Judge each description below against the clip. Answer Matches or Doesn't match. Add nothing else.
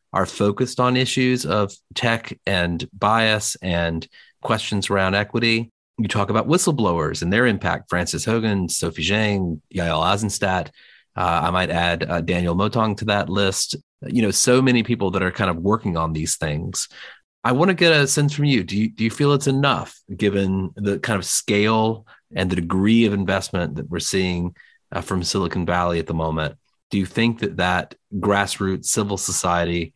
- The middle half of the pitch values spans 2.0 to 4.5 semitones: Matches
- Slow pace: Doesn't match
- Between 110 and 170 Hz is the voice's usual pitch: Doesn't match